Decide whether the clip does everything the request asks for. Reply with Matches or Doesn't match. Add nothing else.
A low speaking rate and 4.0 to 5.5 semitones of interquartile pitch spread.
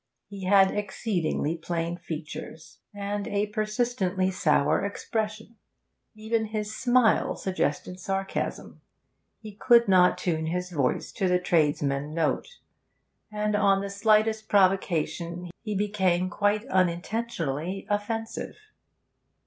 Doesn't match